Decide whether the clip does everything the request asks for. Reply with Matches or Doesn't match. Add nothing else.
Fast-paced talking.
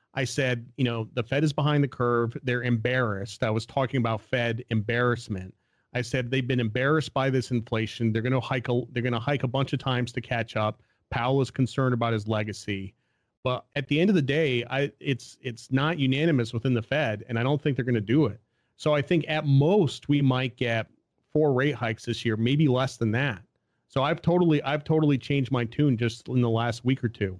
Matches